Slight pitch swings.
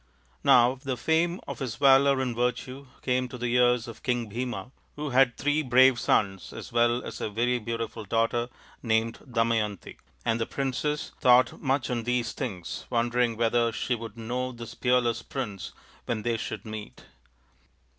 Yes: narrow, 1.9 semitones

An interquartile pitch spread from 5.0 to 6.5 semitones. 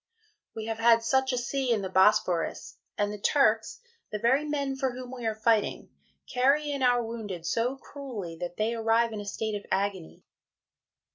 No: average, 3.8 semitones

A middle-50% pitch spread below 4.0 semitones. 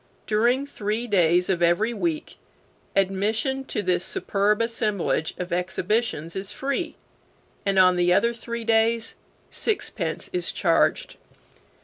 No: average, 4.4 semitones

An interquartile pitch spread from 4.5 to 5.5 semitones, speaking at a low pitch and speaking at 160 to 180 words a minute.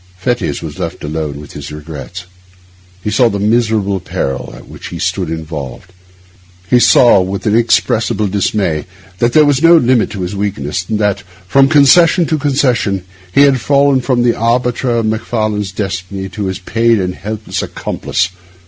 Yes: average, 4.8 semitones; low, 105 Hz; average, 165 wpm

